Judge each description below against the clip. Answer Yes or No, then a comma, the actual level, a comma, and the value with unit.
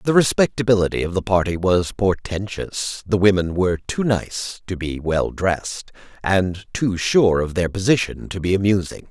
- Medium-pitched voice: No, very low, 95 Hz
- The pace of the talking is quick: No, average, 165 wpm